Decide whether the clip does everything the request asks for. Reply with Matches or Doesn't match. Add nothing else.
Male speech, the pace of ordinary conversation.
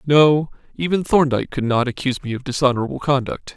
Matches